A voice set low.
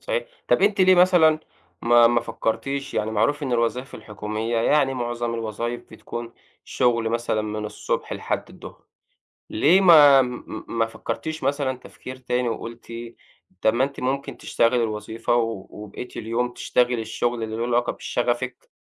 Yes: low, 120 Hz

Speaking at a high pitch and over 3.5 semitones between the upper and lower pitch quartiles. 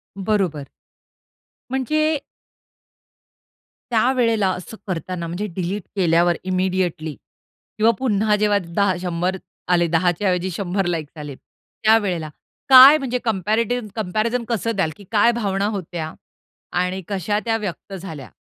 Yes: high, 195 Hz; average, 3.9 semitones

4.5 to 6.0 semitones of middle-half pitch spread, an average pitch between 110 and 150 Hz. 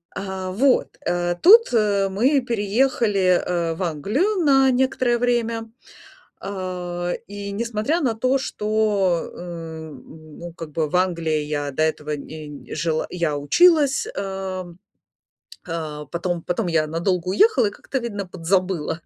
No: wide, 5.6 semitones; medium, 185 Hz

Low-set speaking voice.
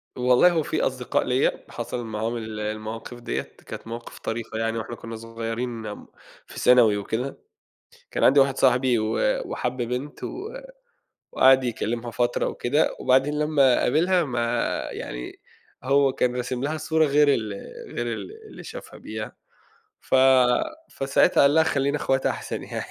Yes: low, 125 Hz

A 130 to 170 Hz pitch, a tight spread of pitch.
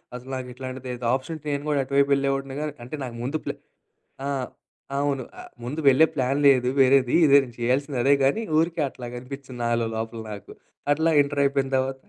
Yes: low, 135 Hz; narrow, 2.1 semitones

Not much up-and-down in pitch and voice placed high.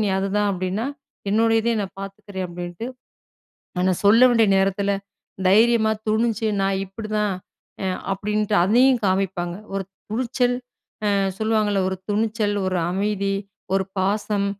Yes: narrow, 2.3 semitones; high, 205 Hz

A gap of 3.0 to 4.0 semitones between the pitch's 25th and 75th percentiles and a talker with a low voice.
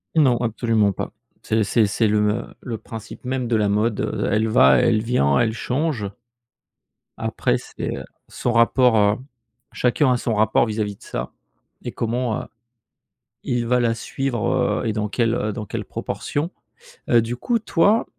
No: narrow, 2.6 semitones; low, 115 Hz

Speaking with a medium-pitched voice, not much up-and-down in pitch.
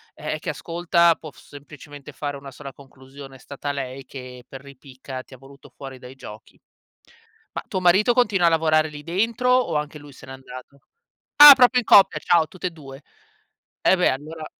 No: medium, 145 Hz; average, 4.1 semitones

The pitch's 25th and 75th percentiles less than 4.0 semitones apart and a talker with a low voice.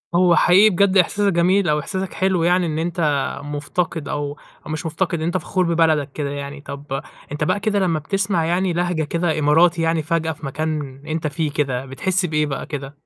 No: average, 3.3 semitones; medium, 160 Hz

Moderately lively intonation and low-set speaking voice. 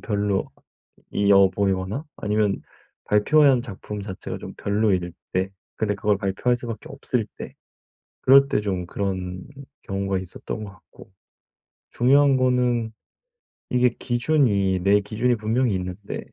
Yes: average, 3.9 semitones; low, 105 Hz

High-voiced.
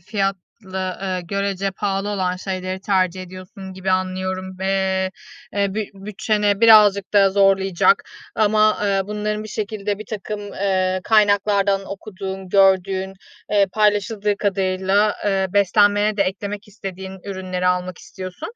Yes: high, 195 Hz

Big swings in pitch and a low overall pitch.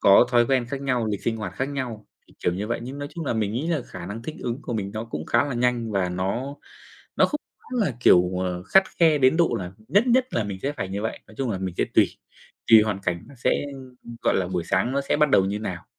Yes: wide, 5.9 semitones; low, 115 Hz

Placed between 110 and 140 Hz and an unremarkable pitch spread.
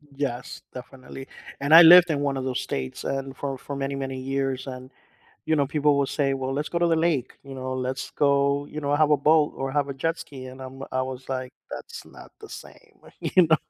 No: low, 135 Hz; narrow, 2.0 semitones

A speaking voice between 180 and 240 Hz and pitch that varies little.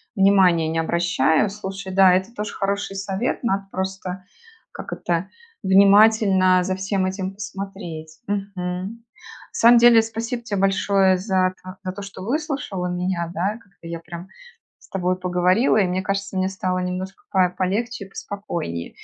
Yes: high, 190 Hz; narrow, 1.7 semitones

